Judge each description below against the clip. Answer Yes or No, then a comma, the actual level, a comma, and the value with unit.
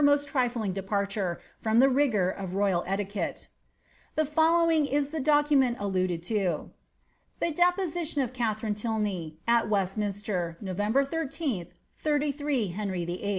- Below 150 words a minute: Yes, average, 140 wpm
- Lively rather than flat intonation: Yes, wide, 6.8 semitones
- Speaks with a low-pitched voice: No, high, 220 Hz